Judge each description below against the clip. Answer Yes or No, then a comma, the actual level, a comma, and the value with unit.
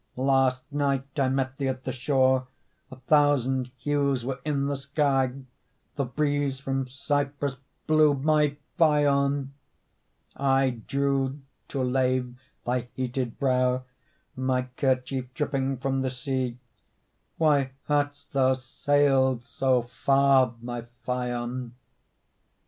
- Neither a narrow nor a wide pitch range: No, narrow, 1.7 semitones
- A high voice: No, low, 135 Hz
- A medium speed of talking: No, slow, 115 wpm